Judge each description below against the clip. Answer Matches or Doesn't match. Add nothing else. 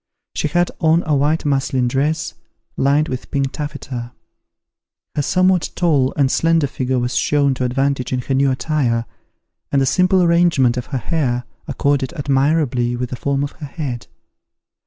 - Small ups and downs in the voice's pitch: Doesn't match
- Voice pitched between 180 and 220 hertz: Doesn't match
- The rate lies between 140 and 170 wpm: Matches